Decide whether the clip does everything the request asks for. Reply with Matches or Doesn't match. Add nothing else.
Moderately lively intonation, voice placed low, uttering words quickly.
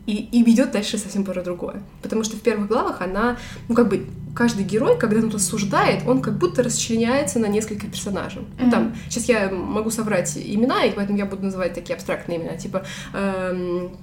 Doesn't match